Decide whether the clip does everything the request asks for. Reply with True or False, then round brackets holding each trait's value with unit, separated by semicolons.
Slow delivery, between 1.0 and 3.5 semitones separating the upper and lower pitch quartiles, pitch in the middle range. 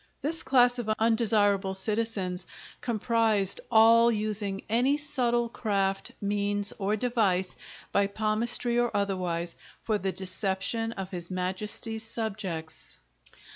False (110 wpm; 3.1 semitones; 210 Hz)